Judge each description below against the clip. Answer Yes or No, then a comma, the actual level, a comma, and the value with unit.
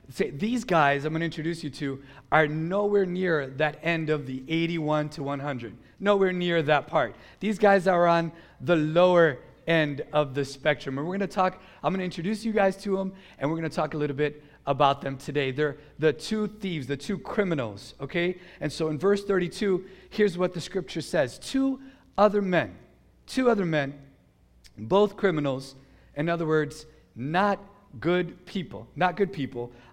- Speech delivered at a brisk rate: No, average, 185 wpm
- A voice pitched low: No, medium, 165 Hz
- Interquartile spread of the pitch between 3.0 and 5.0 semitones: Yes, average, 4.6 semitones